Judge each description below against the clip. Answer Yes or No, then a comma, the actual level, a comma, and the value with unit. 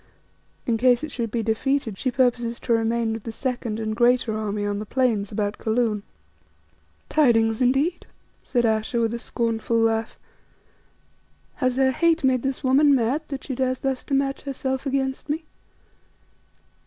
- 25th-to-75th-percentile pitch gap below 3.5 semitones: Yes, average, 3.0 semitones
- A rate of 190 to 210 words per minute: No, average, 160 wpm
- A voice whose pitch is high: Yes, high, 245 Hz